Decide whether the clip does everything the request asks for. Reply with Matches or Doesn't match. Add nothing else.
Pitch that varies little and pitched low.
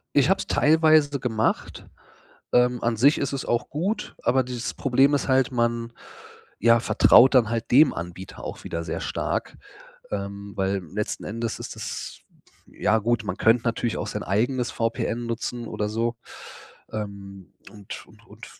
Doesn't match